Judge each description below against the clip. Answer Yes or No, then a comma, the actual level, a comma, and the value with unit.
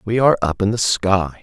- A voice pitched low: Yes, low, 105 Hz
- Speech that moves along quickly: Yes, fast, 250 wpm